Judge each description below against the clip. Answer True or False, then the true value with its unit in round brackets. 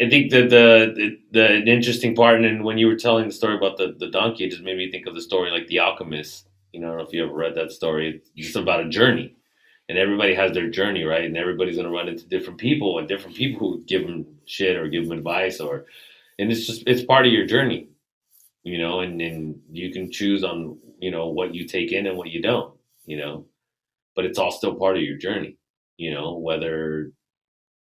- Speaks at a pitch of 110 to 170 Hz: False (95 Hz)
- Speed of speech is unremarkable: False (240 wpm)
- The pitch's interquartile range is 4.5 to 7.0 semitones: True (5.4 semitones)